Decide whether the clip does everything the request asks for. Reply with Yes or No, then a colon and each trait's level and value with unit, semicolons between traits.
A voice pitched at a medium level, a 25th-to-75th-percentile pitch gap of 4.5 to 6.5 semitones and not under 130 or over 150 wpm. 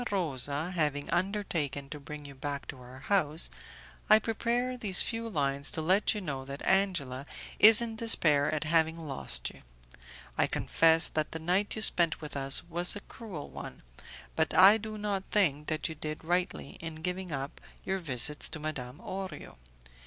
No: medium, 160 Hz; average, 5.2 semitones; average, 175 wpm